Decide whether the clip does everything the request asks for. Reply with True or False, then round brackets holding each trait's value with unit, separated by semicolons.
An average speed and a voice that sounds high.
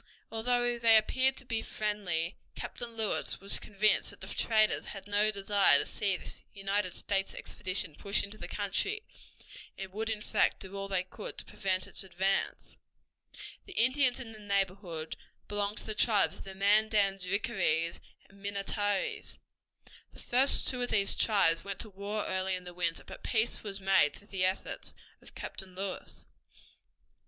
True (165 wpm; 200 Hz)